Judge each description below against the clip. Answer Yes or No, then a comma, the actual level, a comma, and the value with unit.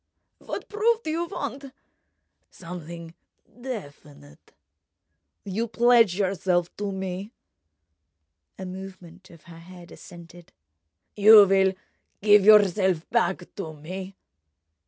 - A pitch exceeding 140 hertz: Yes, high, 190 Hz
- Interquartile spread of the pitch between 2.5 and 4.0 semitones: Yes, average, 3.5 semitones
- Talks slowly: Yes, slow, 100 wpm